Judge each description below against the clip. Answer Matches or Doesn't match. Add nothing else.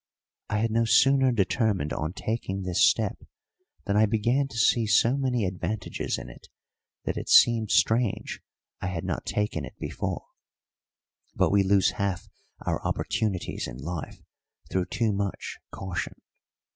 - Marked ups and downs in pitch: Doesn't match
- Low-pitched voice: Matches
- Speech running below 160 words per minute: Matches